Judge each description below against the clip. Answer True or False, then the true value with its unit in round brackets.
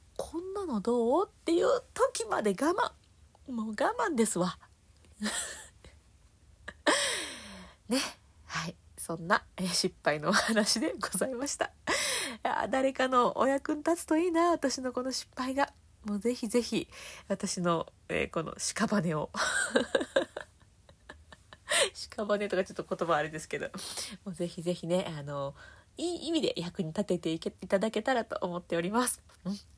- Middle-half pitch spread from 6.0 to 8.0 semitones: True (7.5 semitones)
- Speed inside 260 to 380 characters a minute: False (250 characters per minute)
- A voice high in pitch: True (210 Hz)